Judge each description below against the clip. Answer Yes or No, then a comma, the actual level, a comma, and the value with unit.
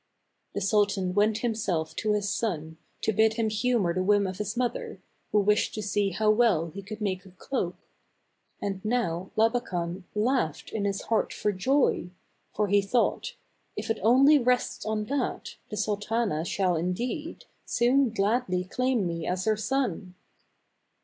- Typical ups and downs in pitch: Yes, average, 3.8 semitones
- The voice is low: No, high, 210 Hz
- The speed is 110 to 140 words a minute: No, average, 160 wpm